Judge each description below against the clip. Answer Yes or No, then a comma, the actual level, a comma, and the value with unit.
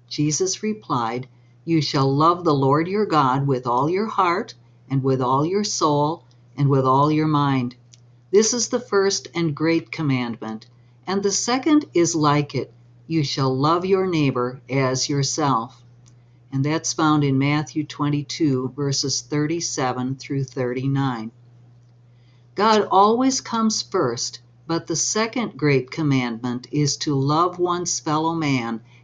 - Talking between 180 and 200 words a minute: No, average, 140 wpm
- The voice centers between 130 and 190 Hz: Yes, medium, 140 Hz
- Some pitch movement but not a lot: Yes, average, 4.9 semitones